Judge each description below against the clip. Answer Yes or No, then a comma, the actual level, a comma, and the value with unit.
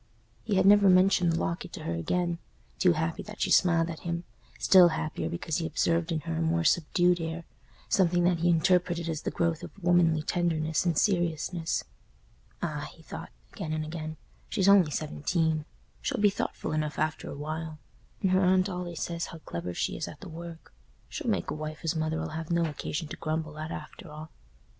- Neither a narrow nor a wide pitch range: No, narrow, 2.0 semitones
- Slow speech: No, average, 195 wpm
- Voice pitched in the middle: Yes, medium, 165 Hz